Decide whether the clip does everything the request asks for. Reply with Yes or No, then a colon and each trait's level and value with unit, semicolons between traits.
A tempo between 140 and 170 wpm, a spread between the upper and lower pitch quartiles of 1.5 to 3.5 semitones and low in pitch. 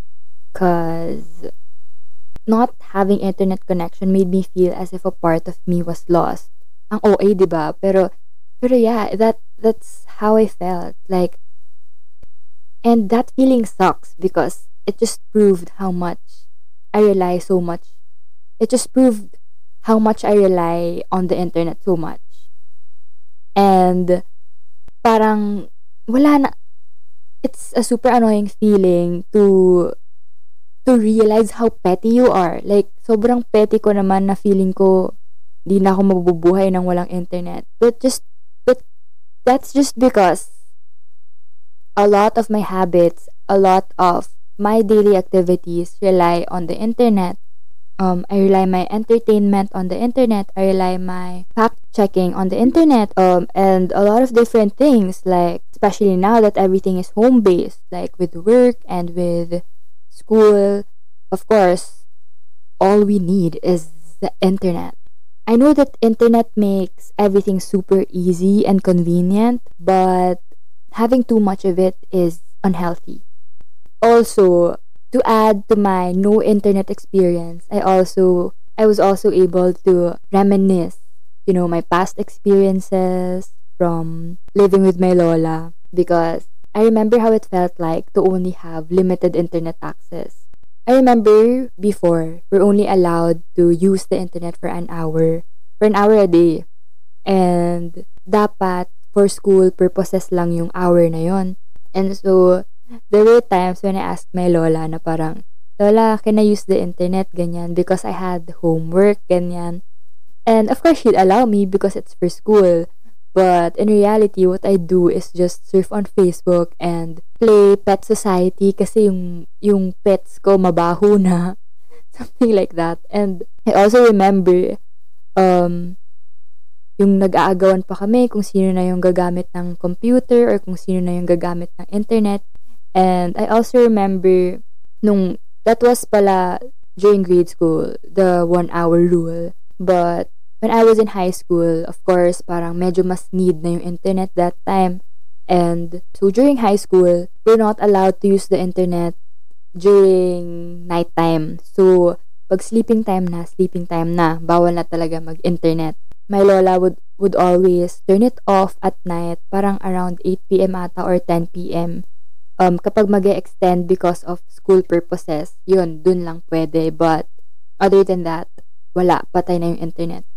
No: average, 145 wpm; average, 2.9 semitones; medium, 185 Hz